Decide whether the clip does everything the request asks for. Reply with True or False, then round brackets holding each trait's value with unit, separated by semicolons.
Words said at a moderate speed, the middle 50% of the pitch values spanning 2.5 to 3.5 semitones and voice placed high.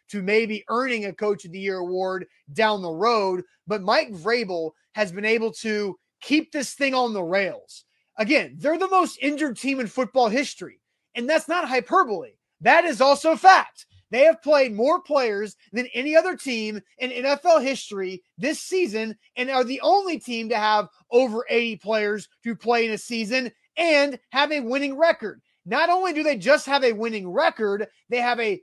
False (185 wpm; 5.6 semitones; 245 Hz)